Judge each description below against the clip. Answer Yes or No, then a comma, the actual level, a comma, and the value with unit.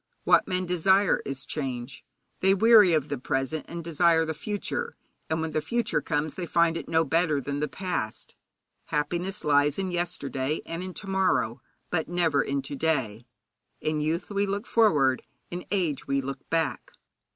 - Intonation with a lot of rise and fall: No, average, 4.2 semitones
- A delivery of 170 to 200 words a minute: Yes, average, 175 wpm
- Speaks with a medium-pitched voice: Yes, medium, 160 Hz